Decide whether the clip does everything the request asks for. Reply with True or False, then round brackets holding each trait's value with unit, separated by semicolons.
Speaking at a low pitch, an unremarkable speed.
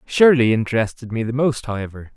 True (120 Hz; 165 wpm)